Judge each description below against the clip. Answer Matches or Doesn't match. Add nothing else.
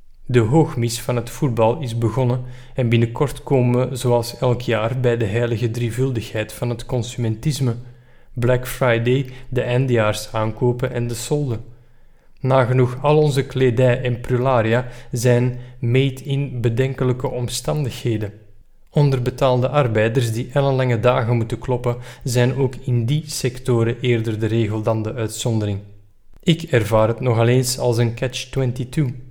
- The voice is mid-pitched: Doesn't match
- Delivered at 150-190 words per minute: Doesn't match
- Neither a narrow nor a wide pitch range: Doesn't match